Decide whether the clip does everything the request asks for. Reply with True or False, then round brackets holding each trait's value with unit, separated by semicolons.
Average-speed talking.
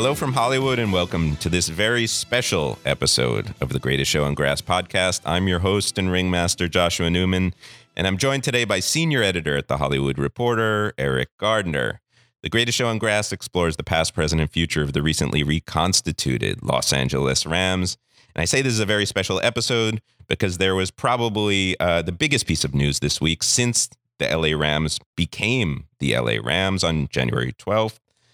True (185 wpm)